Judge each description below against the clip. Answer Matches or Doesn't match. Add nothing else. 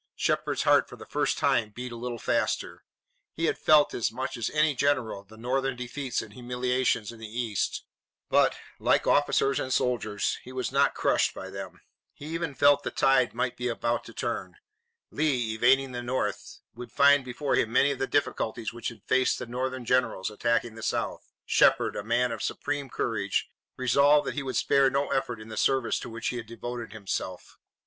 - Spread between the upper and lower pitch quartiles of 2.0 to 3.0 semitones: Matches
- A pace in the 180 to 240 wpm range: Matches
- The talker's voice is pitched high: Doesn't match